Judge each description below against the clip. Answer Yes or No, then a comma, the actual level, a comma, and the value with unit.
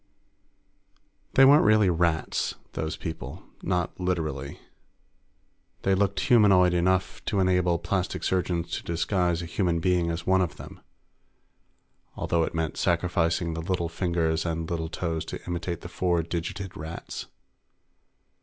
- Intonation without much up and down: Yes, narrow, 1.9 semitones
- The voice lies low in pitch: Yes, very low, 85 Hz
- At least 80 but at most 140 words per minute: Yes, slow, 135 wpm